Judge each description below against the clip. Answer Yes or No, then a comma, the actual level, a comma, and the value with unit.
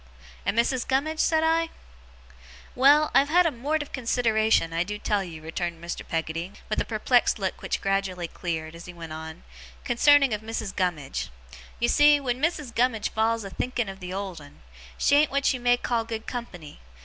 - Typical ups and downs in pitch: No, wide, 6.8 semitones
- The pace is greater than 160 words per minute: Yes, average, 190 wpm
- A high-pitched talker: Yes, high, 225 Hz